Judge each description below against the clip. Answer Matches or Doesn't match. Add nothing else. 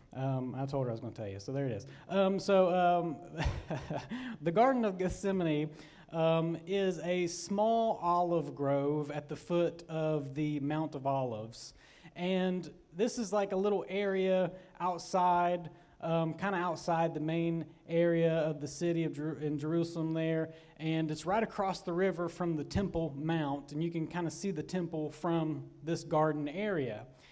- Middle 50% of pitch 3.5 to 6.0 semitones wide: Doesn't match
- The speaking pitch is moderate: Matches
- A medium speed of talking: Matches